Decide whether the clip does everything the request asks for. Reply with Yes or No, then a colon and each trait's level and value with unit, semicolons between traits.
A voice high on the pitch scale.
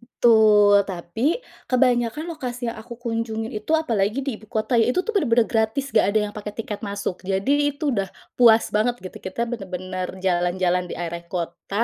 Yes: high, 220 Hz